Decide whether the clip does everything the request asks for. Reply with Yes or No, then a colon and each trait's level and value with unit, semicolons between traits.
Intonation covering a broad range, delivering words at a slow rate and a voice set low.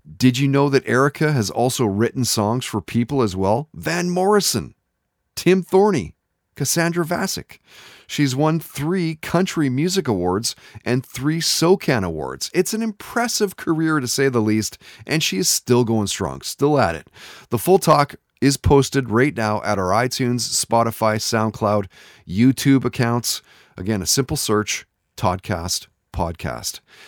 No: wide, 6.4 semitones; average, 145 wpm; low, 125 Hz